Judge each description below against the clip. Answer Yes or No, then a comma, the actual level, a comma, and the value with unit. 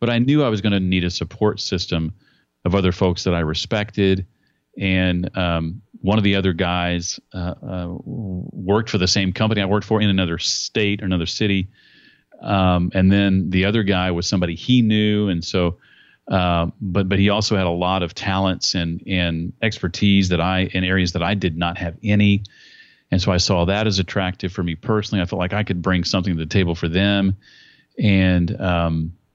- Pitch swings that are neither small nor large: No, narrow, 2.2 semitones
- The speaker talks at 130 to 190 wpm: No, average, 200 wpm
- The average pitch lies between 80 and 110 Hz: Yes, very low, 95 Hz